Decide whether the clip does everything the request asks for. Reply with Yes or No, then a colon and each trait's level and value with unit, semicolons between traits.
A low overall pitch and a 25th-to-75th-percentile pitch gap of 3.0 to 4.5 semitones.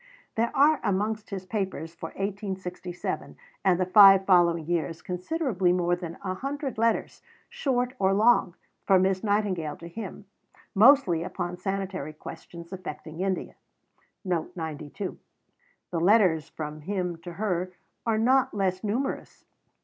No: medium, 185 Hz; average, 3.3 semitones